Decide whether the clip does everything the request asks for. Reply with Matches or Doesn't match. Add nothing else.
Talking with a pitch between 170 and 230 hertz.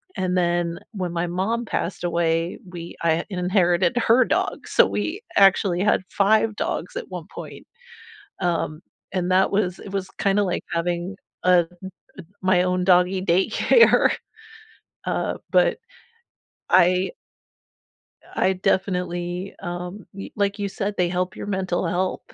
Matches